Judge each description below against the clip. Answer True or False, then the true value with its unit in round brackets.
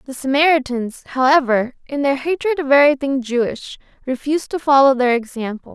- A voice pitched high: True (270 Hz)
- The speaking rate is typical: True (145 wpm)